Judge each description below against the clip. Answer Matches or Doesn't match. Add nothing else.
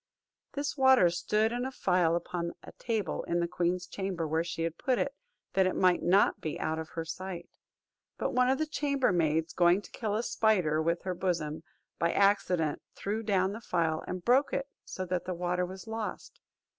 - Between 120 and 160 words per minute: Doesn't match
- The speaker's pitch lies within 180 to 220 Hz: Matches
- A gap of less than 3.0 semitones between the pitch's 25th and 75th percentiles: Doesn't match